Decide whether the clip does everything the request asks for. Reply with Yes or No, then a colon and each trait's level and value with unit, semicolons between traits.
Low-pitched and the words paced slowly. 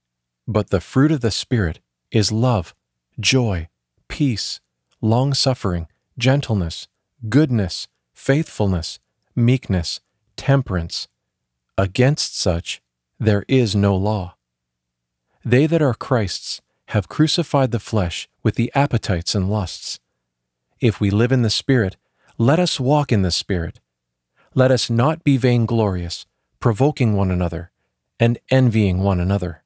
Yes: low, 105 Hz; slow, 120 wpm